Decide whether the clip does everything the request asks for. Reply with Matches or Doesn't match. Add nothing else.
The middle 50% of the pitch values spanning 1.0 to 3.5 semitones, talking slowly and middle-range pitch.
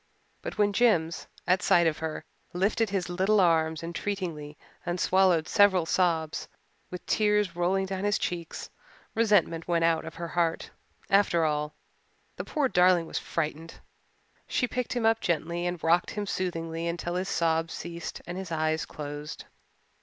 Doesn't match